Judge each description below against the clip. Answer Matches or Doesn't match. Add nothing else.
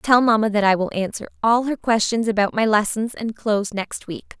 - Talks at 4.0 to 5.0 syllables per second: Doesn't match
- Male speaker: Doesn't match